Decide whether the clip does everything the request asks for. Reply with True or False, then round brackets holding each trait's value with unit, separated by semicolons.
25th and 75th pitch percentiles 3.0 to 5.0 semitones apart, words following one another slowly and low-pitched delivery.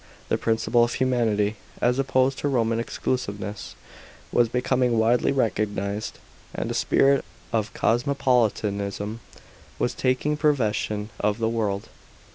True (3.4 semitones; 115 wpm; 115 Hz)